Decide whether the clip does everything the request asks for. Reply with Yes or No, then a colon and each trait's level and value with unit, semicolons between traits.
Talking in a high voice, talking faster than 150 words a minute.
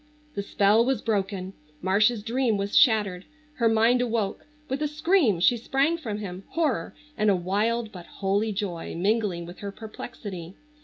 Yes: high, 215 Hz; average, 160 wpm